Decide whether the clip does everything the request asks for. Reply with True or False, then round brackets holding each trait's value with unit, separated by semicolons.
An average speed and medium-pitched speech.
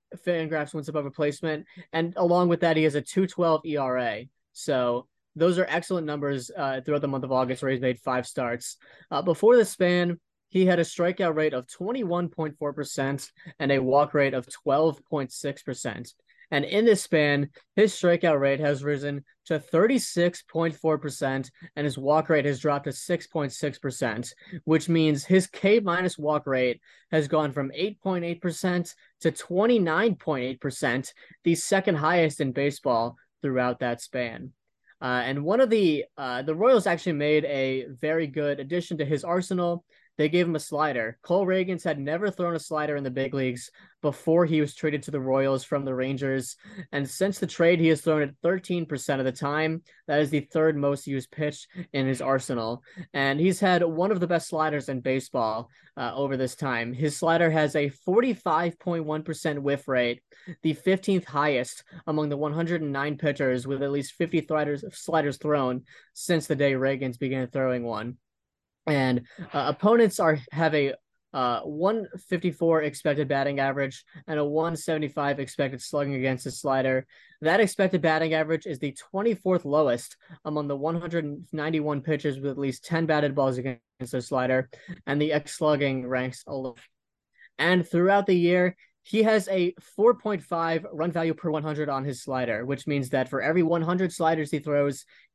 True (185 wpm; 150 Hz)